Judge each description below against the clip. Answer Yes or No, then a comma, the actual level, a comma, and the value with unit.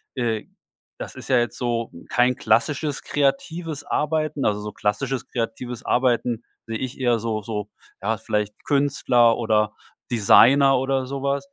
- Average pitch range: Yes, average, 3.4 semitones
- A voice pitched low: Yes, low, 125 Hz